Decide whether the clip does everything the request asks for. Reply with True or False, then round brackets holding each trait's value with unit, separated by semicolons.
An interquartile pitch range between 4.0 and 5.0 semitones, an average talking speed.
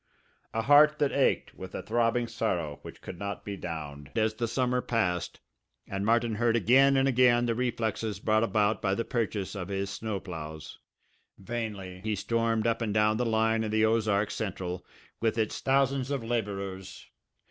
False (3.1 semitones; 175 wpm)